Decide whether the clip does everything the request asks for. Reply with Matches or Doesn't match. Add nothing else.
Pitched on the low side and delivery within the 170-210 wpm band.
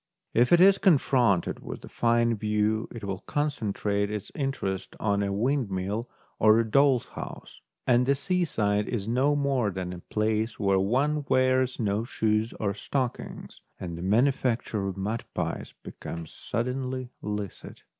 Doesn't match